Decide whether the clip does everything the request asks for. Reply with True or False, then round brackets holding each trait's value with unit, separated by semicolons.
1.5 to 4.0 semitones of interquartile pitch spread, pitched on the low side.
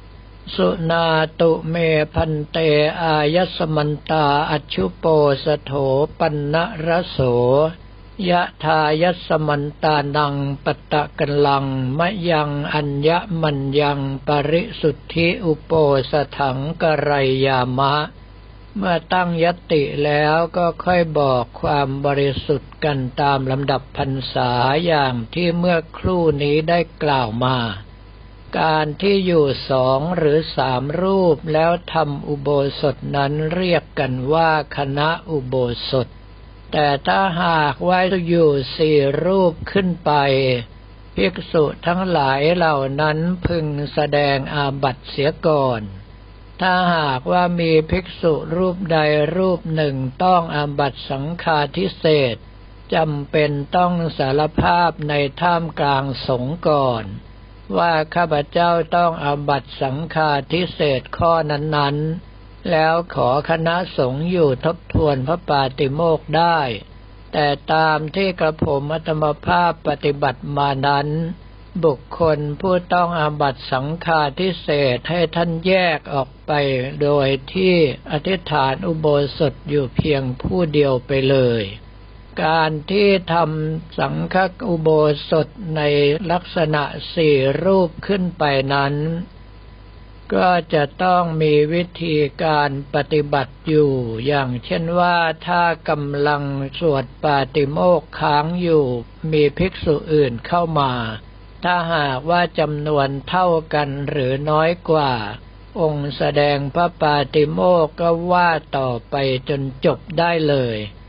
False (3.2 semitones; 150 Hz)